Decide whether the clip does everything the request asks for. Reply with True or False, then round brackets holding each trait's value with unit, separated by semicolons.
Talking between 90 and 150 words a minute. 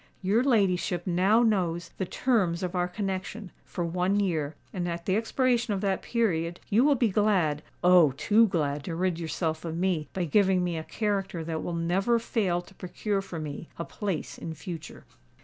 False (185 wpm)